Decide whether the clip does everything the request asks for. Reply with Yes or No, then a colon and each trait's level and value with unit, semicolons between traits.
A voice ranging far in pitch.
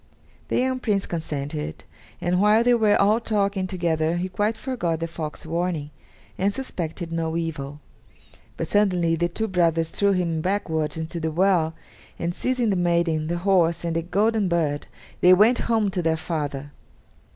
No: average, 3.7 semitones